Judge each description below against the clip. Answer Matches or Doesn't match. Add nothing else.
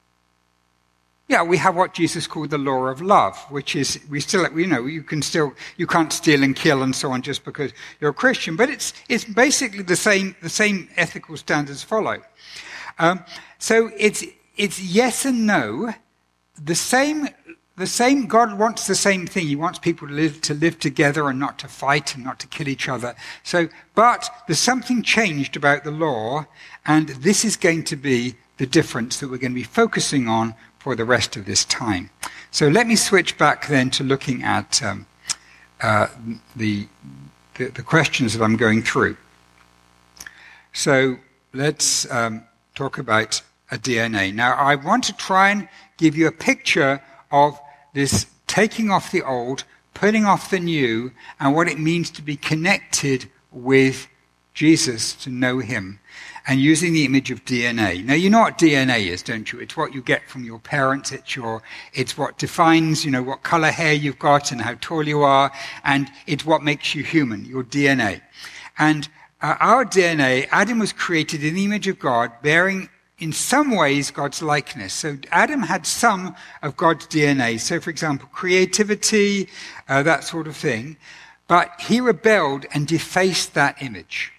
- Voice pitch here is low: Doesn't match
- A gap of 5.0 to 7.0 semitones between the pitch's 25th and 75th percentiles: Matches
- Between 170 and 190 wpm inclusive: Matches